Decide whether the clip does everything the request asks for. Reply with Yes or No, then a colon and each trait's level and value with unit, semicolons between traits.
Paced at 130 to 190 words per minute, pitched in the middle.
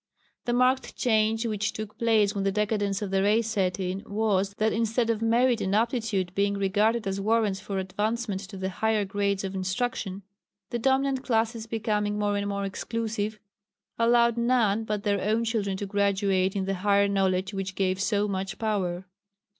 No: average, 180 wpm; high, 205 Hz